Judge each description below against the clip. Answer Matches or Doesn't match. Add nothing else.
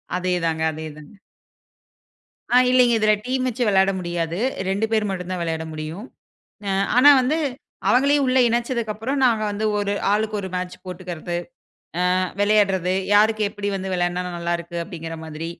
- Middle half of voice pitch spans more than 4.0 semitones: Matches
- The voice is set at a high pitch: Matches